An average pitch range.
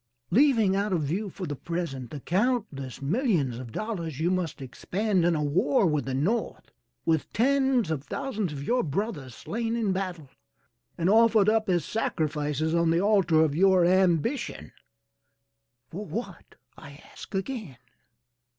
No: wide, 6.2 semitones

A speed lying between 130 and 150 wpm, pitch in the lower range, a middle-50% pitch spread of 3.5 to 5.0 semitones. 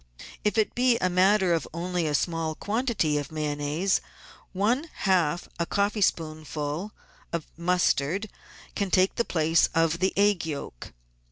No: average, 140 wpm; medium, 175 Hz; average, 4.2 semitones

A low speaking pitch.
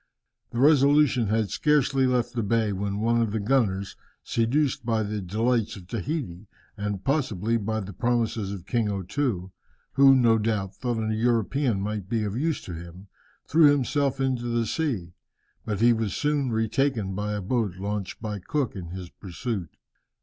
Yes: low, 110 Hz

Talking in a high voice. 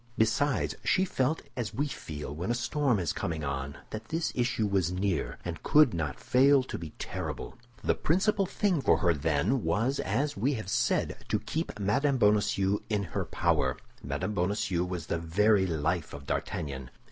No: low, 105 Hz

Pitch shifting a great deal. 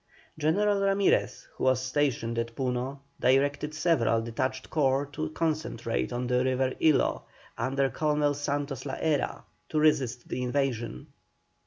No: average, 3.2 semitones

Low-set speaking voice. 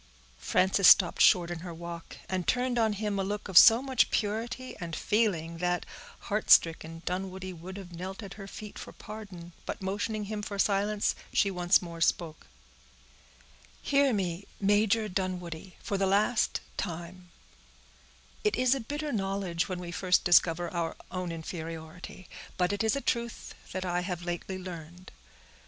No: medium, 185 Hz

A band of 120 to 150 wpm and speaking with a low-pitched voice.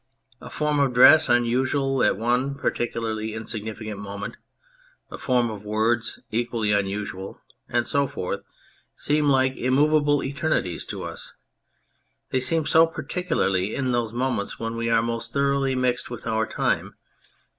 Yes: average, 140 wpm; low, 120 Hz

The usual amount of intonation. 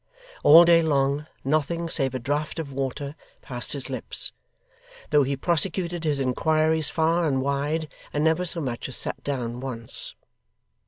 Yes: average, 3.1 semitones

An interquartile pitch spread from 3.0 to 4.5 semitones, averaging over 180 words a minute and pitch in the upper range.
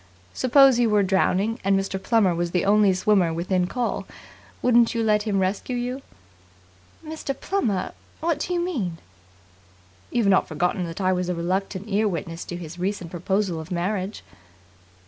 No: average, 4.1 semitones; average, 165 wpm; high, 195 Hz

